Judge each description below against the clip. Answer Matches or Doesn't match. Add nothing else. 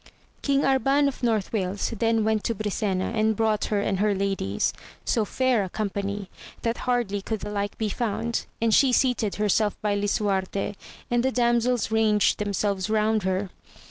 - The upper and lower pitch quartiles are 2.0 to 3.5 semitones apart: Matches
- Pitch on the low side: Doesn't match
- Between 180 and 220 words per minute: Doesn't match